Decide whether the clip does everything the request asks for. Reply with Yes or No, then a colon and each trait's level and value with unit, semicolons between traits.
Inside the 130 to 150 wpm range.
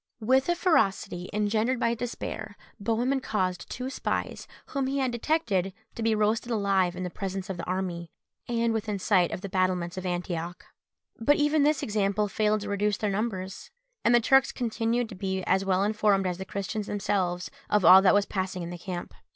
No: average, 190 wpm